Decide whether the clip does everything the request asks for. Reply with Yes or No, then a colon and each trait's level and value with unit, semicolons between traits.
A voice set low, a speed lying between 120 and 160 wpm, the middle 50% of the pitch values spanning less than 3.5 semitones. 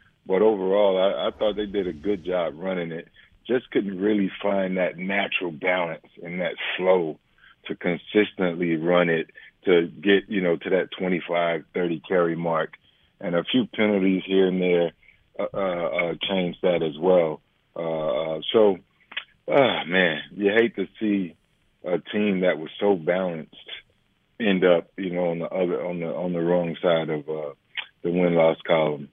No: very low, 90 Hz; average, 170 wpm; average, 2.7 semitones